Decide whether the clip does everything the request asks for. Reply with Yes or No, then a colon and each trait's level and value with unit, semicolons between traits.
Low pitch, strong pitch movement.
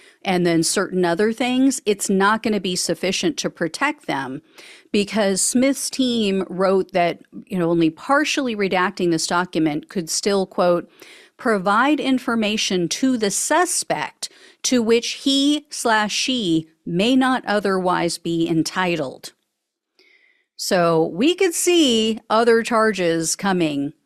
No: high, 210 Hz; wide, 6.9 semitones